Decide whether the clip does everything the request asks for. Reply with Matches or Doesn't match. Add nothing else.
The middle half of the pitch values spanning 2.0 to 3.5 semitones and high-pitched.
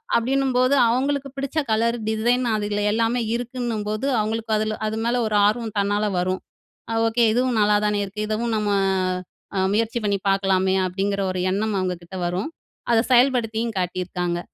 Matches